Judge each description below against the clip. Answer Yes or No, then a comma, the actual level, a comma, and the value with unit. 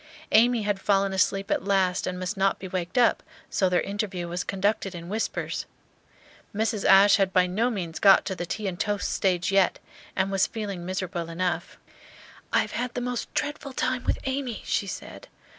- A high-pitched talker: Yes, high, 195 Hz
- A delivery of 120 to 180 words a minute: No, average, 190 wpm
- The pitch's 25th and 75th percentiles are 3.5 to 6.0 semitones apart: No, average, 3.0 semitones